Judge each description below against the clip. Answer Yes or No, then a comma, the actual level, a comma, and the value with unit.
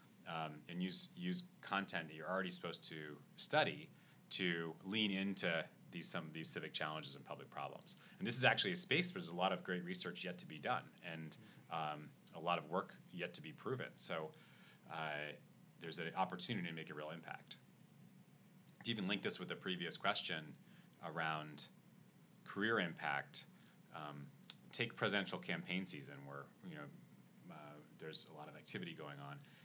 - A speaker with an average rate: Yes, average, 175 wpm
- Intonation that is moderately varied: Yes, average, 3.8 semitones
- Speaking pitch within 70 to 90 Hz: Yes, very low, 85 Hz